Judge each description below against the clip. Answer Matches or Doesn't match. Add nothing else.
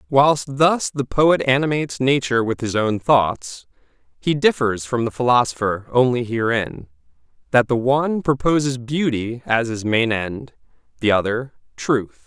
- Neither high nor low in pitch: Doesn't match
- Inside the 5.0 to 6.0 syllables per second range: Doesn't match